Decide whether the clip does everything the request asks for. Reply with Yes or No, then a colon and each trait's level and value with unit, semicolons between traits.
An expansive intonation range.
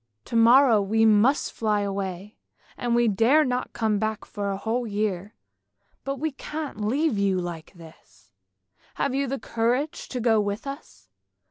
No: average, 3.9 semitones